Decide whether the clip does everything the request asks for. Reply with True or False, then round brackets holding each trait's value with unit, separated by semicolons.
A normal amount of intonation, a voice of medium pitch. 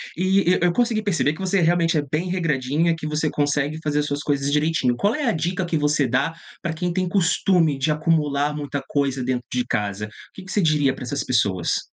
True (3.7 semitones; 155 Hz)